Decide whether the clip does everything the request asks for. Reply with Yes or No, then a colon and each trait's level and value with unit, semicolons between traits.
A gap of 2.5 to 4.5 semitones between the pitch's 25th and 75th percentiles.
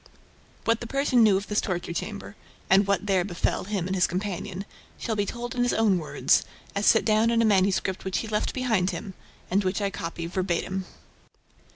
Yes: average, 2.9 semitones